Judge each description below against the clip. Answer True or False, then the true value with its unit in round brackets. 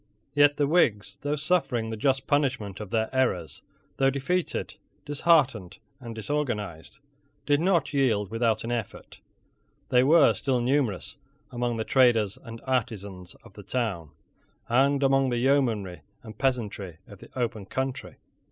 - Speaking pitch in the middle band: False (120 Hz)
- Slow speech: False (145 wpm)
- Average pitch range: True (4.4 semitones)